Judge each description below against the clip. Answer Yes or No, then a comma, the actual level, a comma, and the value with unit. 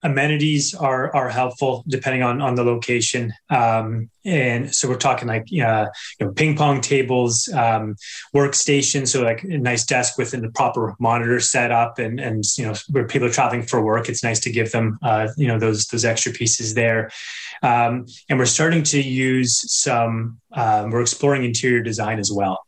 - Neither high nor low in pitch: No, low, 120 Hz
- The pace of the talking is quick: No, average, 185 wpm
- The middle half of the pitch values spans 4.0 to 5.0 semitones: No, average, 2.9 semitones